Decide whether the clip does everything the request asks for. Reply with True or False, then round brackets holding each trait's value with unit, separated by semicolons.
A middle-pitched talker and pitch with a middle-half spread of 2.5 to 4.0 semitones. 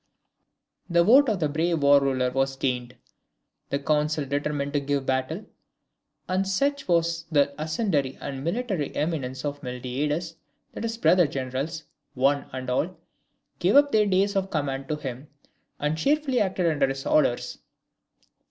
False (150 Hz; 4.9 semitones)